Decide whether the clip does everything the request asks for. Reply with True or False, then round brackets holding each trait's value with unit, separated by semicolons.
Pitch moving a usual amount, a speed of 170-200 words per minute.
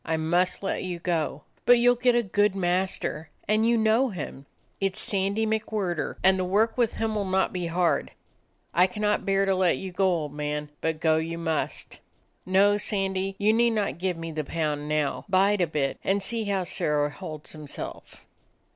True (4.2 semitones; 195 wpm)